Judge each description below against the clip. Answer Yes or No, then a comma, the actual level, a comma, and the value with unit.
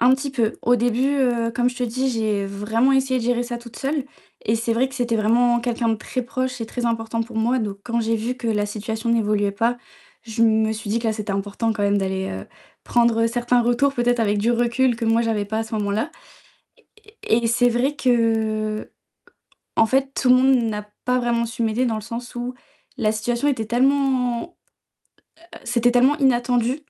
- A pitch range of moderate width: No, narrow, 2.0 semitones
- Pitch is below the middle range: No, high, 235 Hz